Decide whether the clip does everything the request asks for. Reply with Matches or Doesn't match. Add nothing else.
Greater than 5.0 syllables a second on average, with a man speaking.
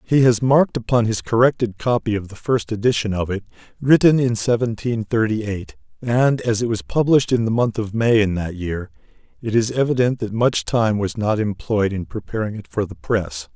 Matches